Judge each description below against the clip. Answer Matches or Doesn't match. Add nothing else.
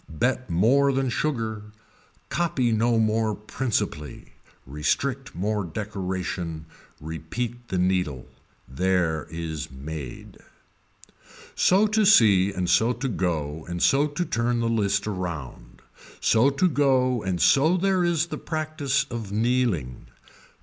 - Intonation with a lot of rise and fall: Matches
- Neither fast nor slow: Doesn't match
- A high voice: Doesn't match